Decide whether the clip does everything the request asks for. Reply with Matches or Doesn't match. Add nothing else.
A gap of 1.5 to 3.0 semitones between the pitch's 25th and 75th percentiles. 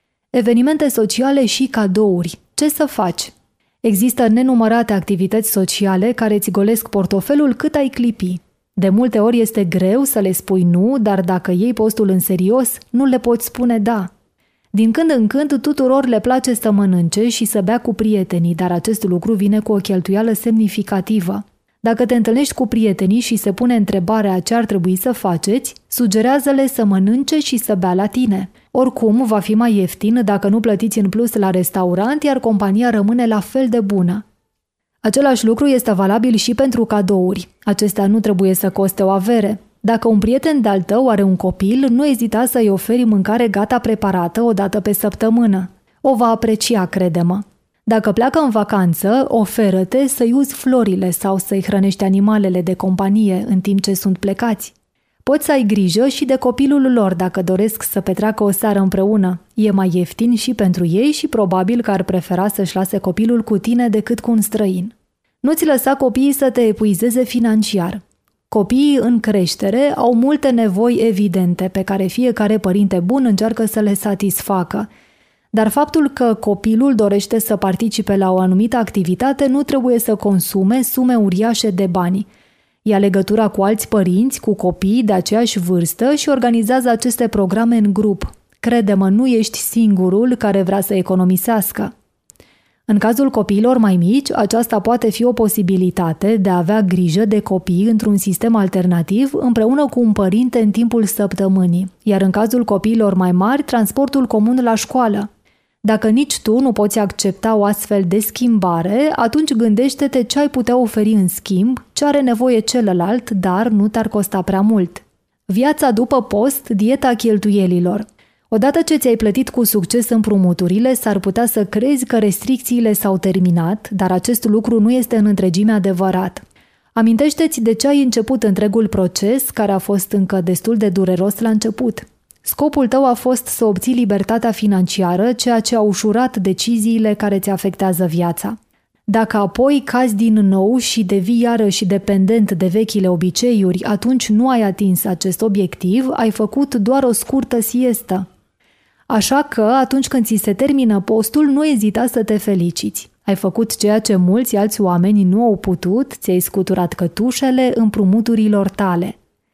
Doesn't match